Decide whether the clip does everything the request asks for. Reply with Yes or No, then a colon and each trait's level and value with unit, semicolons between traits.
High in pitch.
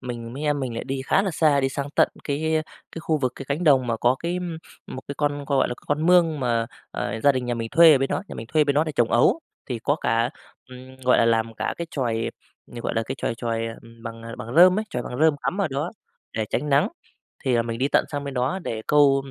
No: low, 135 Hz